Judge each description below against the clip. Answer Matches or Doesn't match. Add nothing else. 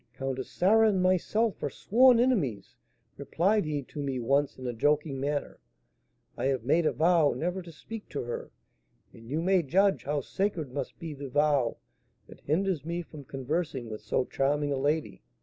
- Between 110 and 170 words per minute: Doesn't match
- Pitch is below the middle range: Doesn't match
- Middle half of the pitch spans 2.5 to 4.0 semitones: Doesn't match